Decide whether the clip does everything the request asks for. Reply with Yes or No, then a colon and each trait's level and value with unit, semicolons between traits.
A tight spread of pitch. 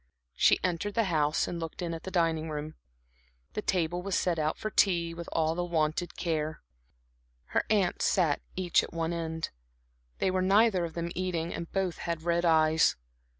Yes: narrow, 2.1 semitones